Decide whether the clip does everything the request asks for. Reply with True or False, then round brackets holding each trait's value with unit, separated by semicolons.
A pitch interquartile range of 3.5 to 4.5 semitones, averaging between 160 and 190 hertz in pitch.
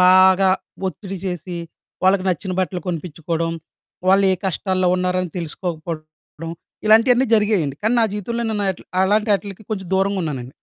False (2.9 semitones; 185 Hz)